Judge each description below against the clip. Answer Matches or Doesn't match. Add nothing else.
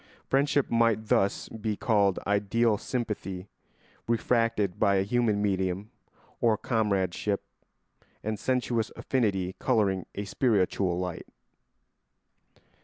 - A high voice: Doesn't match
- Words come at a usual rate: Doesn't match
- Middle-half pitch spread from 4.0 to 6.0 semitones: Doesn't match